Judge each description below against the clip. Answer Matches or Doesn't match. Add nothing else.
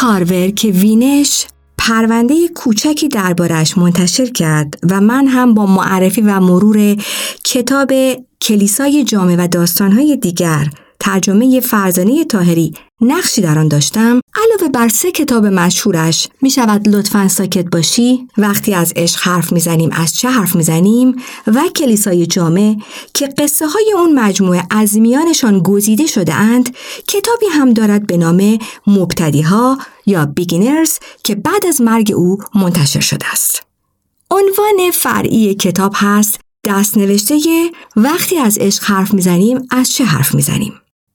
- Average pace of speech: Matches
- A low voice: Doesn't match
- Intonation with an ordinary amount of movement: Doesn't match